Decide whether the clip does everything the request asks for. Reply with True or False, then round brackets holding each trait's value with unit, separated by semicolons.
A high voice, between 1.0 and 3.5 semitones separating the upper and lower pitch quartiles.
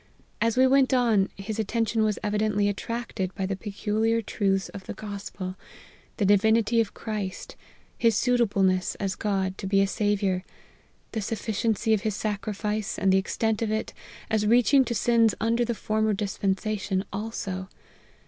True (210 Hz; 2.4 semitones)